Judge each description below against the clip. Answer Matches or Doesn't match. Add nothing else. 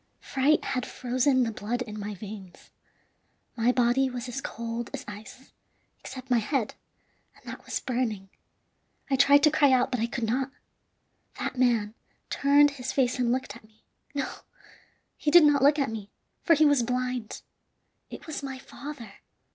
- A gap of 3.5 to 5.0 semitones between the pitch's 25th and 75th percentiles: Doesn't match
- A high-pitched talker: Matches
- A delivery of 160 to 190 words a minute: Matches